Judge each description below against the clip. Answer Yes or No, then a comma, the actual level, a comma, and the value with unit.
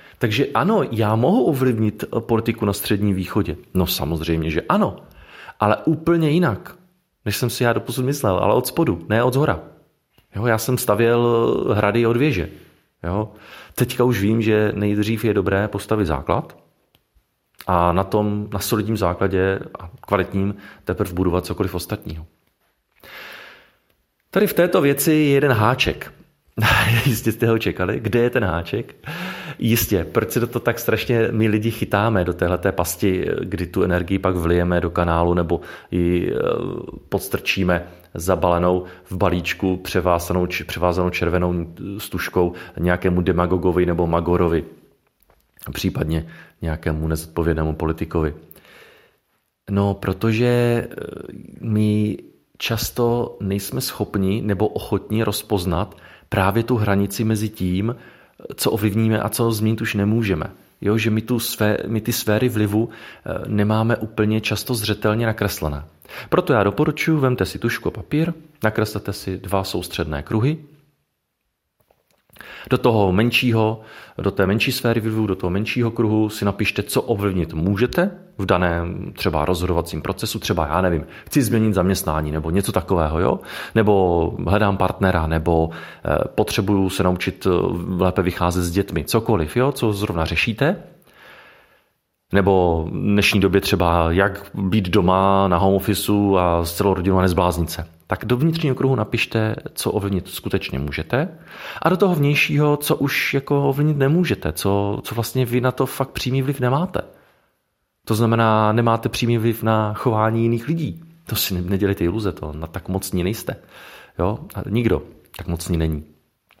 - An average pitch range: Yes, average, 4.4 semitones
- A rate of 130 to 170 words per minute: Yes, average, 140 wpm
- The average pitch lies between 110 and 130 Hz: No, low, 100 Hz